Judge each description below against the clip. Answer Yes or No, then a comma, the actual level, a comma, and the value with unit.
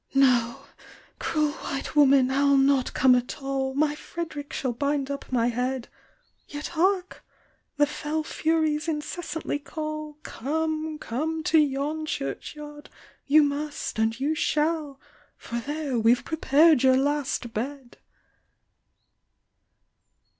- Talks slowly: Yes, slow, 120 wpm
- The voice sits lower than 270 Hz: No, very high, 290 Hz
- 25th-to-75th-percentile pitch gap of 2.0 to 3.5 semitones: Yes, narrow, 2.6 semitones